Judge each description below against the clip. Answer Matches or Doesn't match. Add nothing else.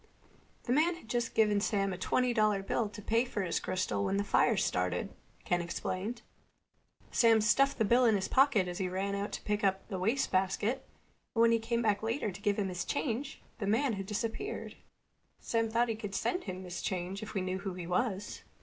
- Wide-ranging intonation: Doesn't match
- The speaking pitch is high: Matches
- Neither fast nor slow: Doesn't match